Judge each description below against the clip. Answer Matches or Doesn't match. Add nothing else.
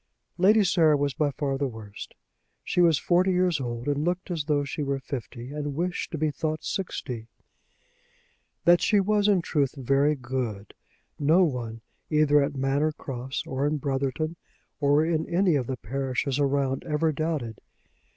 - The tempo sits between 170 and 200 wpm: Doesn't match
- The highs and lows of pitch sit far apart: Doesn't match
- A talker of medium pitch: Matches